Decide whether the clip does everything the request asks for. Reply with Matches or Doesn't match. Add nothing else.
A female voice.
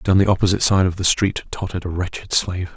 Doesn't match